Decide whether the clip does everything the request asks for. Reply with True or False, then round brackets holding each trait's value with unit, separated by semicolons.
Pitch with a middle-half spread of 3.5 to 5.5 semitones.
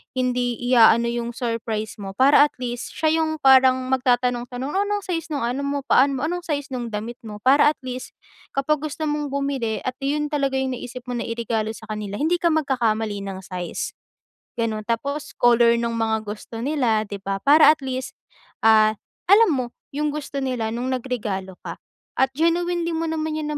True (4.3 semitones)